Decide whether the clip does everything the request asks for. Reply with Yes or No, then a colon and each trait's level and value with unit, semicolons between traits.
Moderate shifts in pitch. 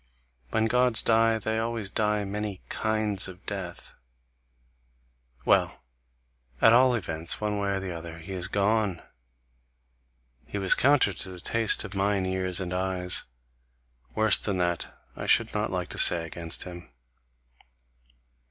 Yes: average, 3.3 semitones